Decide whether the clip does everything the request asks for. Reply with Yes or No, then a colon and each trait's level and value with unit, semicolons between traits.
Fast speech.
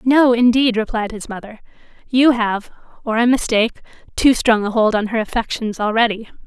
No: average, 165 wpm